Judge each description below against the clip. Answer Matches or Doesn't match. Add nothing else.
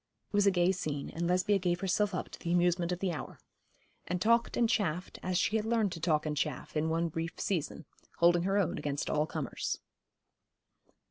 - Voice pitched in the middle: Matches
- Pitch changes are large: Doesn't match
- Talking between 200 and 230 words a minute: Matches